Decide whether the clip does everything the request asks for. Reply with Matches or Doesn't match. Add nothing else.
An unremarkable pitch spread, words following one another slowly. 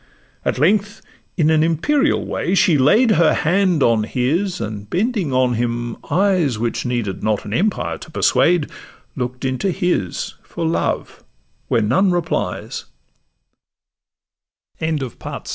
Doesn't match